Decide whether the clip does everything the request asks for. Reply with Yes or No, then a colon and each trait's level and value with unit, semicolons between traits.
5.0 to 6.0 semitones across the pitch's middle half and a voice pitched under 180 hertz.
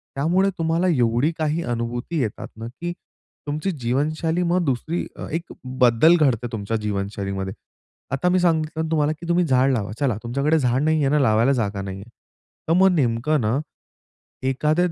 Yes: wide, 5.6 semitones; medium, 140 Hz